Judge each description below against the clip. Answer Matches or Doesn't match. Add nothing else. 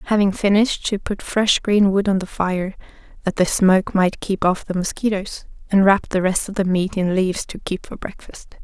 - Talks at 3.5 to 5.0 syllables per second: Doesn't match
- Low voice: Doesn't match